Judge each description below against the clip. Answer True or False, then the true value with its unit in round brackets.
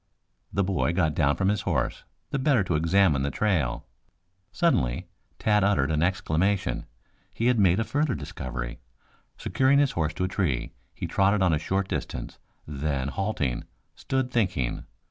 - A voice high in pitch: False (95 Hz)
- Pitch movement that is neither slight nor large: False (5.9 semitones)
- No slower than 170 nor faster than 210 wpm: False (160 wpm)